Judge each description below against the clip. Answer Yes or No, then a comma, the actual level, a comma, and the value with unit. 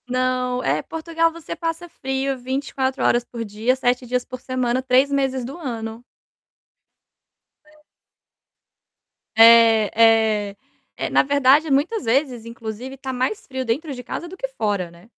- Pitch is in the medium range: No, very high, 255 Hz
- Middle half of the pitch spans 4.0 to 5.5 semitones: No, average, 3.4 semitones